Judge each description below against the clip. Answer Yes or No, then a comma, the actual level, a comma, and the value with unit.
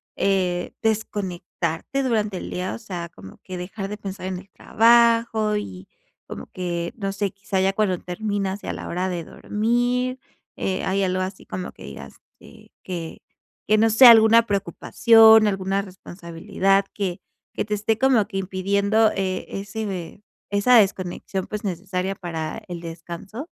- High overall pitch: Yes, high, 195 Hz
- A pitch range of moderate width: Yes, average, 3.0 semitones